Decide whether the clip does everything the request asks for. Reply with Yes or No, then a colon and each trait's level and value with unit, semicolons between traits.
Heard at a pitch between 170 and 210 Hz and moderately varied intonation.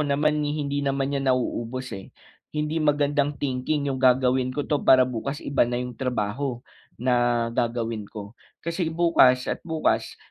No: low, 130 Hz; average, 3.0 semitones